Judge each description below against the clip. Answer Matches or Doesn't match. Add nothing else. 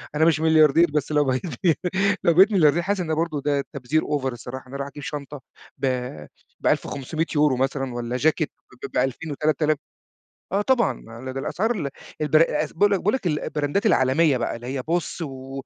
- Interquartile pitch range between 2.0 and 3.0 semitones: Doesn't match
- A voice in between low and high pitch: Matches